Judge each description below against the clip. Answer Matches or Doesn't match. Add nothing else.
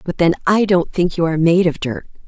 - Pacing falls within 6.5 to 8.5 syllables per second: Doesn't match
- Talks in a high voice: Doesn't match